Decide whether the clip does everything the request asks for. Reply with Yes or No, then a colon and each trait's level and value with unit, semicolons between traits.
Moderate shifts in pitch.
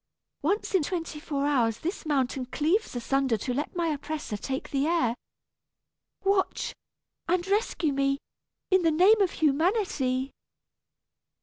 Yes: average, 4.8 semitones